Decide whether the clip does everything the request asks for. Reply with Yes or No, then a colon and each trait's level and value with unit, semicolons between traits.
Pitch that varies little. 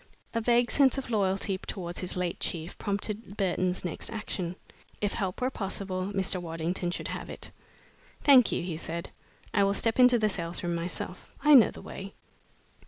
No: average, 3.8 semitones